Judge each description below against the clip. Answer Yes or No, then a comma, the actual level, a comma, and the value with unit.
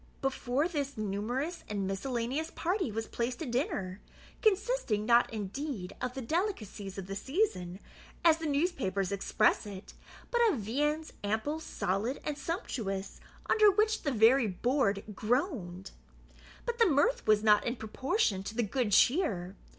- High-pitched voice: Yes, high, 245 Hz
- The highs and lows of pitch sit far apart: Yes, wide, 7.5 semitones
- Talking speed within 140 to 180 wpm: Yes, average, 145 wpm